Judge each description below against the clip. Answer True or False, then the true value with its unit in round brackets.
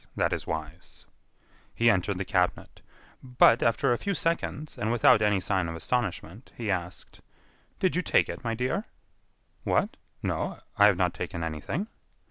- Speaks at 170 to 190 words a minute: False (155 wpm)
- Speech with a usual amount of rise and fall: False (5.8 semitones)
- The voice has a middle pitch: False (105 Hz)